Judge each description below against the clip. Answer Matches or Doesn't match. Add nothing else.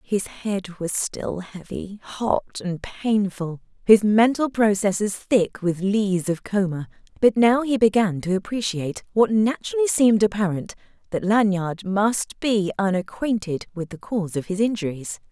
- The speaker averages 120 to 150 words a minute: Matches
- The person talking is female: Matches